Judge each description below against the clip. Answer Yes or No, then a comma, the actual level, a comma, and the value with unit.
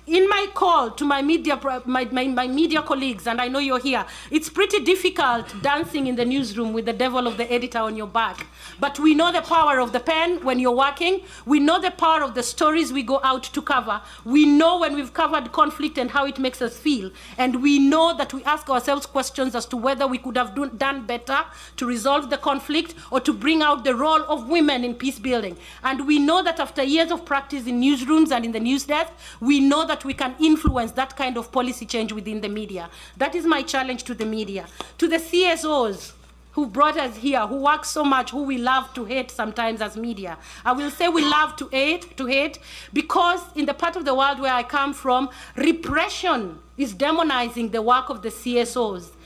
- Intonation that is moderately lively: Yes, average, 3.6 semitones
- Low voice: No, very high, 275 Hz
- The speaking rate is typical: No, fast, 220 wpm